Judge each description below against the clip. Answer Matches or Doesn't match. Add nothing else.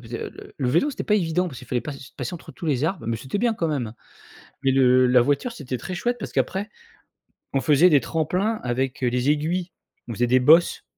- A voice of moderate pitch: Matches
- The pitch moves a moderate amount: Doesn't match